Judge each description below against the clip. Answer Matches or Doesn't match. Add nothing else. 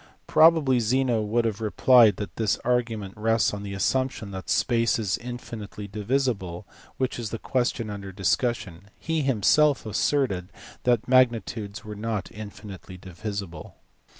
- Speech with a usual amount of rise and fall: Matches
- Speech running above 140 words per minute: Doesn't match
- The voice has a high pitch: Doesn't match